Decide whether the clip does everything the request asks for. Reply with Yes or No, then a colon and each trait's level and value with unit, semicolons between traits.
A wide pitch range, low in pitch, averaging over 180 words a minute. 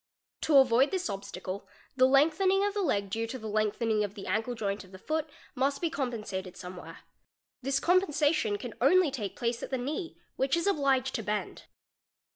No: wide, 6.2 semitones; very high, 255 Hz; average, 190 wpm